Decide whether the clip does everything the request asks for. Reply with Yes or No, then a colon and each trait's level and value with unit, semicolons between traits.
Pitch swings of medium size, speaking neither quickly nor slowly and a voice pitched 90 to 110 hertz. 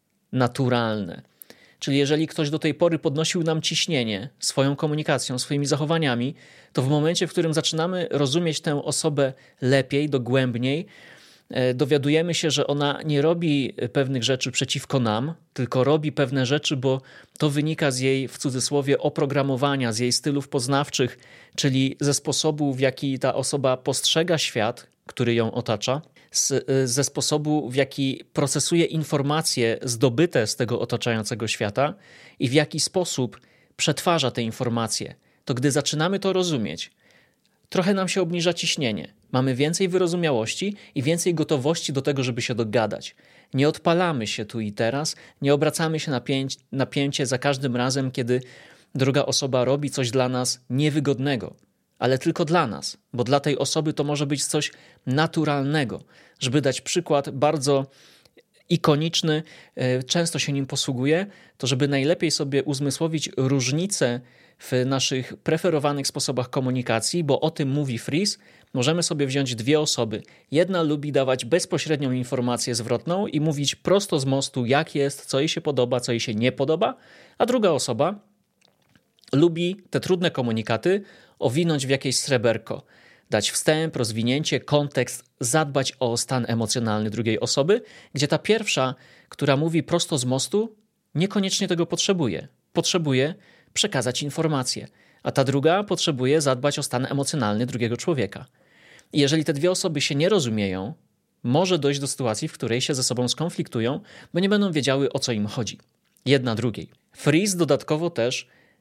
No: average, 3.7 semitones; average, 145 wpm; medium, 140 Hz